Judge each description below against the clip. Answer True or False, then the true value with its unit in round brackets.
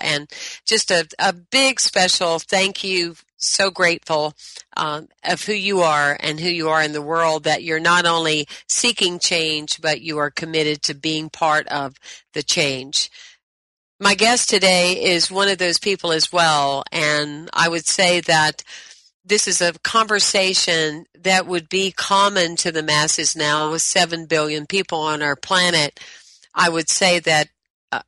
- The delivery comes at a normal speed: True (160 wpm)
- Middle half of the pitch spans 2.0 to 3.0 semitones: False (3.4 semitones)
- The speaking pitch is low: False (165 Hz)